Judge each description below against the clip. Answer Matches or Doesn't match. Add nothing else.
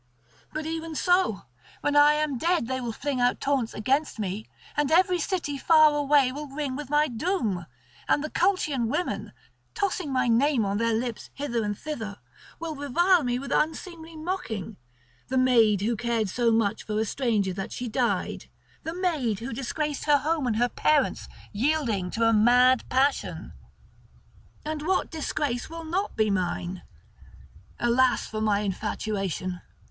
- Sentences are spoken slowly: Doesn't match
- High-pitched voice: Matches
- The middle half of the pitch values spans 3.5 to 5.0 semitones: Doesn't match